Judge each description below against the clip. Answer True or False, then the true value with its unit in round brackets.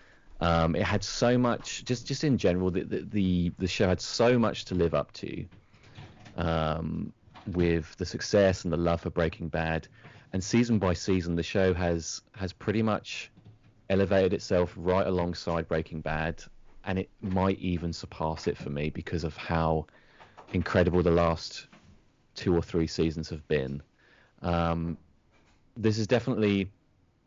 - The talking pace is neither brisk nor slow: True (155 wpm)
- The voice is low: True (90 Hz)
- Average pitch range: True (3.7 semitones)